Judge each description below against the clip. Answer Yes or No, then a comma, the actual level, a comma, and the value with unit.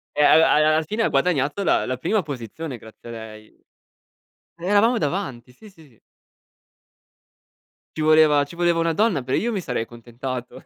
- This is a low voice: No, medium, 150 Hz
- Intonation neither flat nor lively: No, wide, 5.7 semitones